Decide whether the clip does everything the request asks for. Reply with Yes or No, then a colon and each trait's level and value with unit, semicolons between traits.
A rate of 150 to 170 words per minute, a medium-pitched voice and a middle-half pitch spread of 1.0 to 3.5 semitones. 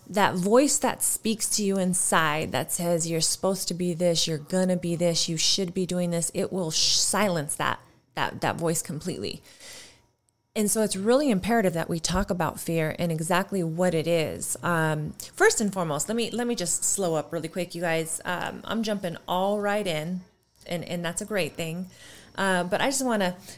No: average, 200 wpm; medium, 180 Hz; average, 3.2 semitones